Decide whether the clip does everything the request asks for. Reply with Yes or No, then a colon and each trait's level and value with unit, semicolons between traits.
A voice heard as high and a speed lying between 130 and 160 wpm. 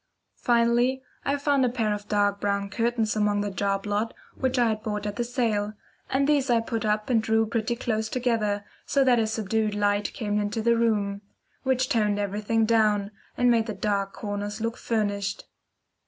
No: high, 220 Hz; average, 185 wpm